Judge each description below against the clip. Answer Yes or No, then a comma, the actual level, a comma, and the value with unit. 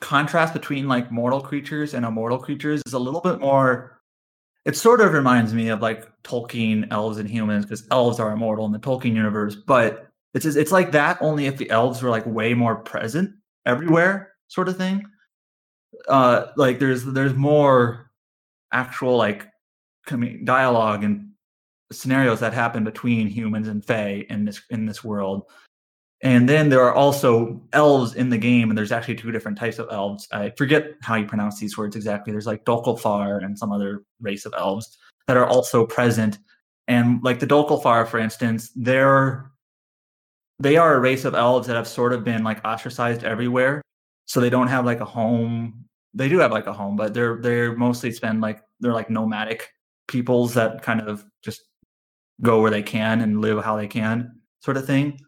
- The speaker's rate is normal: Yes, average, 185 wpm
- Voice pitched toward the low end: Yes, low, 115 Hz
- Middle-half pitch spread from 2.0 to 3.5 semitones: Yes, average, 3.1 semitones